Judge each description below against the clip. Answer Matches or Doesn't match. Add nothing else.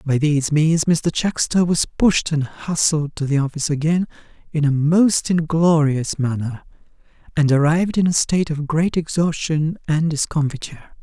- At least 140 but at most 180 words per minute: Matches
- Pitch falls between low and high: Matches